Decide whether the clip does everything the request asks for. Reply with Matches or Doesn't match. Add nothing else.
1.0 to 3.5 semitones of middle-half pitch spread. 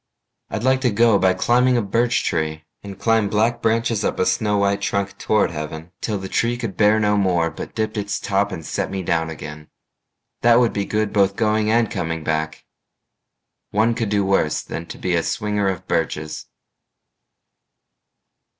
Doesn't match